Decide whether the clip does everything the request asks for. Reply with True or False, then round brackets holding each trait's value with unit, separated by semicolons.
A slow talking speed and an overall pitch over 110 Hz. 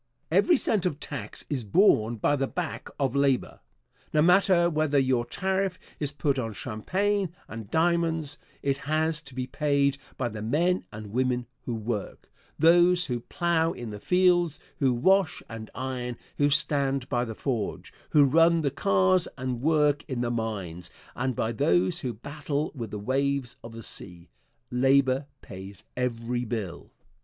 False (160 wpm; 135 Hz)